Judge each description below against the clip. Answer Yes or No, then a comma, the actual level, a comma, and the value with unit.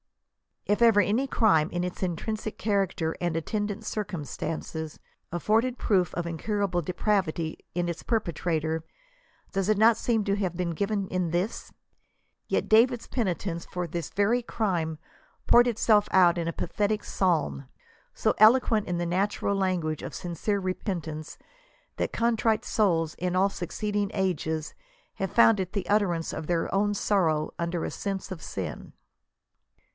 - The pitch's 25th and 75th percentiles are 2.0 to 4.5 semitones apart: Yes, average, 3.7 semitones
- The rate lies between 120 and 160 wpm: Yes, average, 150 wpm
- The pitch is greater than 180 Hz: Yes, high, 190 Hz